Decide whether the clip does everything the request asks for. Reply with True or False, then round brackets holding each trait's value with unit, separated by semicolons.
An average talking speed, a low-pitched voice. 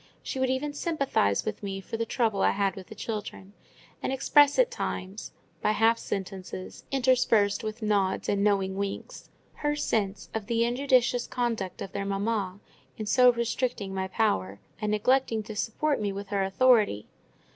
False (170 wpm; 215 Hz)